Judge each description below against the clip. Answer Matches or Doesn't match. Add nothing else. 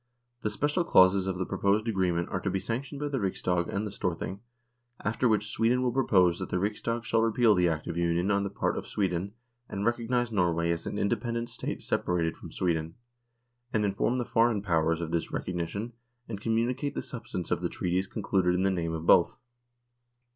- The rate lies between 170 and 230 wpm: Matches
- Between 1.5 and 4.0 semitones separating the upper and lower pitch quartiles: Doesn't match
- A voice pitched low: Matches